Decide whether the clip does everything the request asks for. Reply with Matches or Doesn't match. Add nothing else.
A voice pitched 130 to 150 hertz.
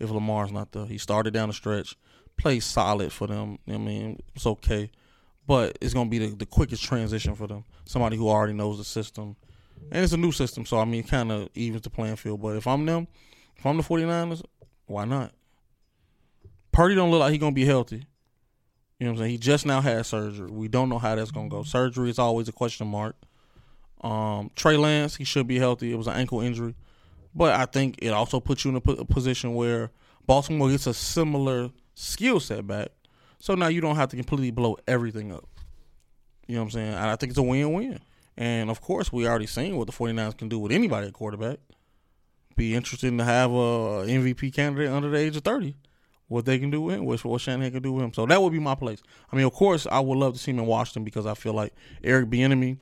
Doesn't match